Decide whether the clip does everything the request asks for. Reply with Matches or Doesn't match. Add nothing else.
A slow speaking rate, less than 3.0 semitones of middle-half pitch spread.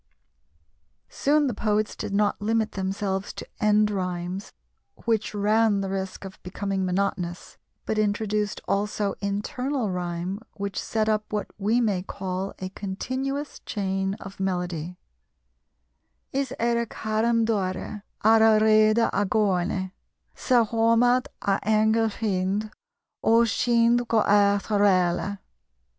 Matches